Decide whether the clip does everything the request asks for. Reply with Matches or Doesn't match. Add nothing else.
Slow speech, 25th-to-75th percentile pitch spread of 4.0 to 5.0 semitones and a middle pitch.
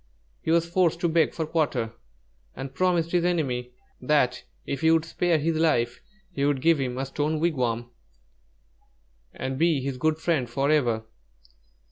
Doesn't match